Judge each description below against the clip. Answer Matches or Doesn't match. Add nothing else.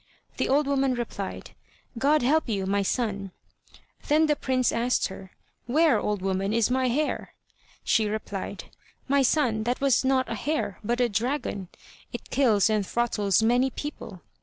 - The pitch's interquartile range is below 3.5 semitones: Doesn't match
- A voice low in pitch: Doesn't match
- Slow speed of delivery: Doesn't match